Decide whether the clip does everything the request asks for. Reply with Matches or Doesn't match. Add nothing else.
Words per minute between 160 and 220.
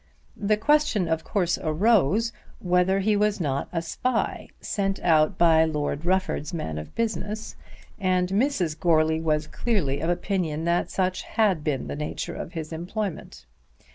Doesn't match